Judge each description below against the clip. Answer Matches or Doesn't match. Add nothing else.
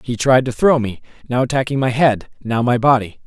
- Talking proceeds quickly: Matches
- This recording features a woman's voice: Doesn't match